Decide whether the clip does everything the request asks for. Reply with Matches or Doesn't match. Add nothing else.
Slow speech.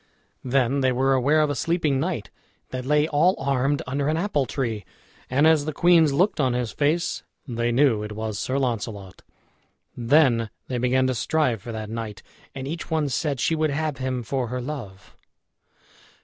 Doesn't match